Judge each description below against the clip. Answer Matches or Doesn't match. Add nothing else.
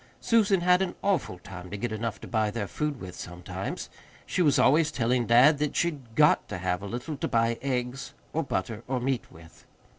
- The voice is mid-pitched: Doesn't match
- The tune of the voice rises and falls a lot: Matches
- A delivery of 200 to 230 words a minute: Matches